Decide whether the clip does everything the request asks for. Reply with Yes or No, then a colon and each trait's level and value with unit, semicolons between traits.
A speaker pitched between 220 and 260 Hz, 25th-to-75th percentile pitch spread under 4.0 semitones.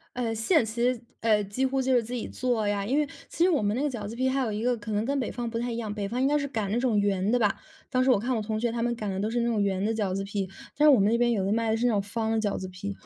Yes: high, 225 Hz; average, 3.2 semitones